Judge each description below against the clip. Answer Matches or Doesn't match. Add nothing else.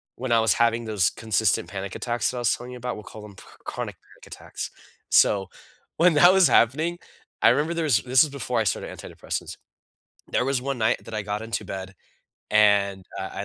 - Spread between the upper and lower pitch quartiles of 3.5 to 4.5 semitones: Matches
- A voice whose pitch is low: Matches